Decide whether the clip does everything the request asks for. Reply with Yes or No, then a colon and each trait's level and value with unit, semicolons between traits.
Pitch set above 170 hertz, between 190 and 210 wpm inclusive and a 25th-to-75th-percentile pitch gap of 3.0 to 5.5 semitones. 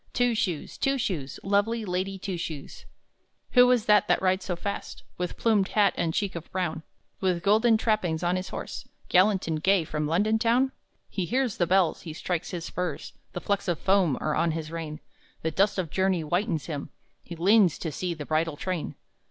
Yes: medium, 185 Hz; average, 195 wpm; average, 3.8 semitones